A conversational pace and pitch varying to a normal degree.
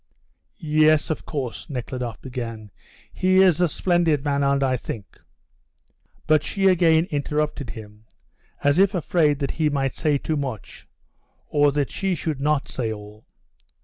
Yes: average, 150 wpm; average, 3.7 semitones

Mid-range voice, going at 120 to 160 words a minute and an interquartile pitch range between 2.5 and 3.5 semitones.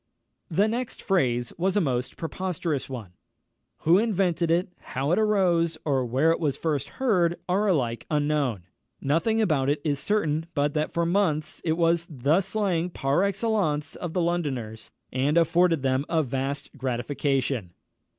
No: medium, 160 Hz; average, 155 wpm; average, 4.7 semitones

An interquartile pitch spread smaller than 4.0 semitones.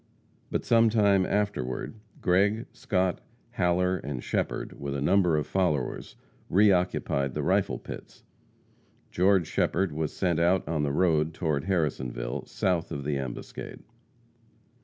No: average, 4.7 semitones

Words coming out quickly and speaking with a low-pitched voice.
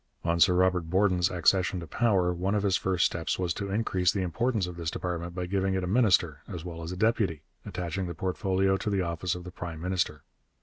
Yes: fast, 225 wpm; very low, 90 Hz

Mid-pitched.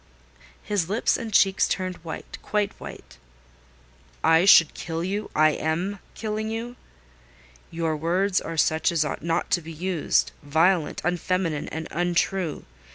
Yes: medium, 175 Hz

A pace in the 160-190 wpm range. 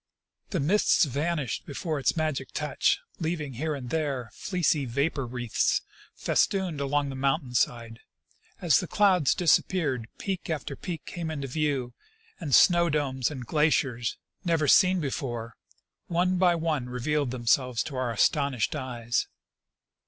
No: slow, 135 wpm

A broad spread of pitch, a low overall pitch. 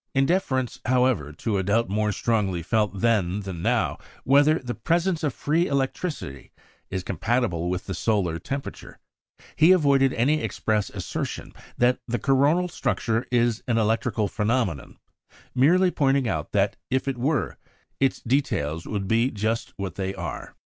Yes: wide, 5.7 semitones; low, 115 Hz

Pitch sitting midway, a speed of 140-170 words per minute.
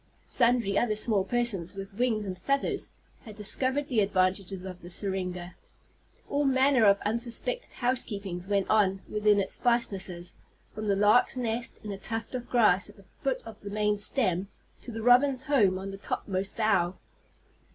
No: high, 210 Hz; average, 165 wpm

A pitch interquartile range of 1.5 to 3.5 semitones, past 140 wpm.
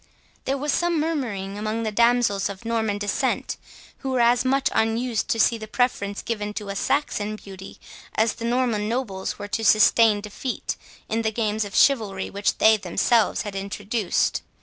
Yes: average, 2.9 semitones; average, 170 wpm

